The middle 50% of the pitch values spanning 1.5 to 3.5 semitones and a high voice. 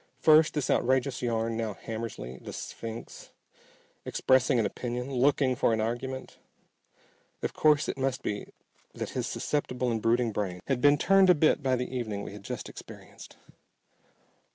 No: average, 3.2 semitones; low, 125 Hz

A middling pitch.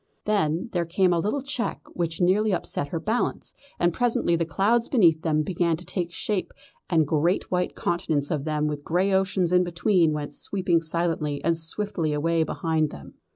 Yes: medium, 170 Hz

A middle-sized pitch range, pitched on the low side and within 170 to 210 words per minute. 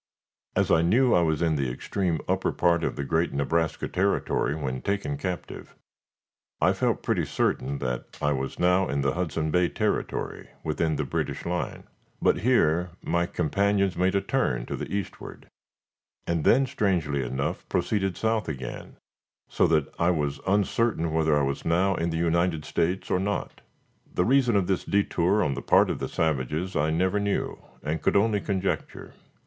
Yes: average, 4.3 semitones; very low, 85 Hz; average, 175 wpm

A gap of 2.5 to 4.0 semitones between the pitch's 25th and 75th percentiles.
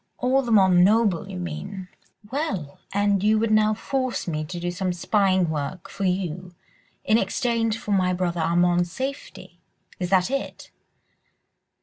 Yes: average, 3.5 semitones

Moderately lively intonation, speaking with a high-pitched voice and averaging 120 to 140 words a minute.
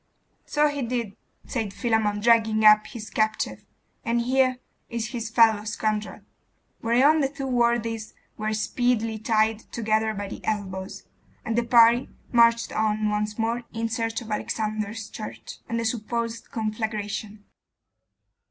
No: narrow, 1.6 semitones; high, 225 Hz; slow, 135 wpm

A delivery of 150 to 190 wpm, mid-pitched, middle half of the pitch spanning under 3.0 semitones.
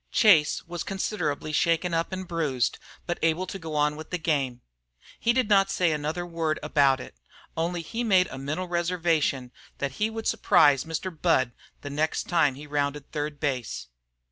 No: average, 175 wpm; medium, 160 Hz; average, 3.4 semitones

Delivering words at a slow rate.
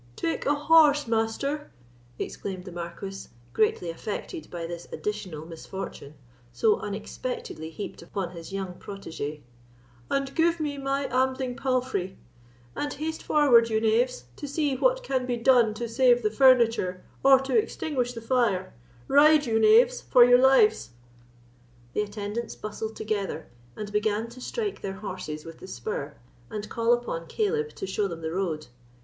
No: average, 150 wpm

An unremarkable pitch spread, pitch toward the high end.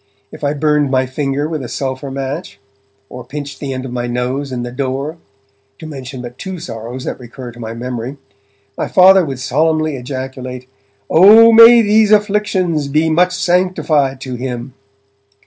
No: average, 4.2 semitones; medium, 140 Hz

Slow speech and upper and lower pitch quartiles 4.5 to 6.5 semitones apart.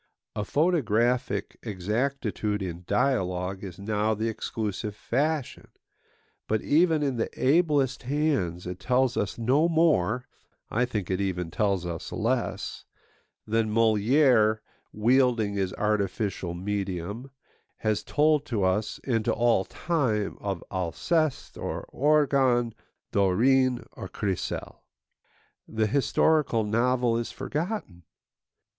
Yes: slow, 110 wpm; average, 5.1 semitones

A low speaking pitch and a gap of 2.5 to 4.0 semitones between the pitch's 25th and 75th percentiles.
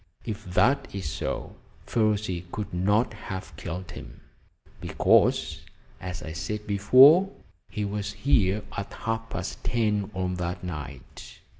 Yes: low, 100 Hz; average, 3.0 semitones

